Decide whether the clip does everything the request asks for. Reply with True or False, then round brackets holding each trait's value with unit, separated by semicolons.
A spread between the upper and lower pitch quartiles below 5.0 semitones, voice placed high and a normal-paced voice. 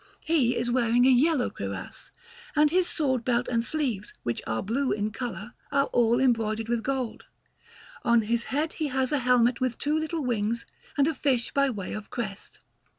True (3.4 semitones; 245 Hz; 185 wpm)